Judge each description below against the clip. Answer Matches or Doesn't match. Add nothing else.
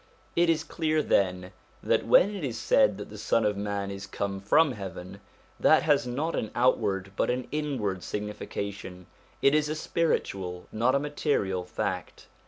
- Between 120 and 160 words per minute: Doesn't match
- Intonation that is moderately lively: Doesn't match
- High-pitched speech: Doesn't match